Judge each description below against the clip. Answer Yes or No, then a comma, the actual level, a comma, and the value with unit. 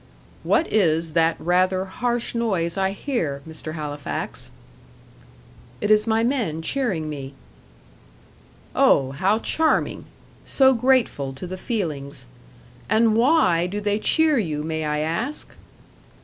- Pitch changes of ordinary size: No, wide, 6.8 semitones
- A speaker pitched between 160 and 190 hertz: Yes, medium, 185 Hz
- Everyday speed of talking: No, slow, 120 wpm